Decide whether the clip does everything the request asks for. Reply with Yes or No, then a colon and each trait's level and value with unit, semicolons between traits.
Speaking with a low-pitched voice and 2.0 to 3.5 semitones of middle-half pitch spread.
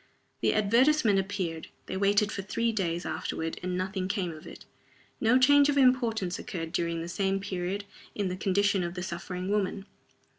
No: high, 195 Hz; average, 2.9 semitones